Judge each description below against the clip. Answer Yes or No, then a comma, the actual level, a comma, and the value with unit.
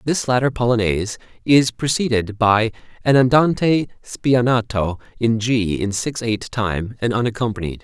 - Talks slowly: Yes, slow, 130 wpm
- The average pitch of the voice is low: Yes, low, 115 Hz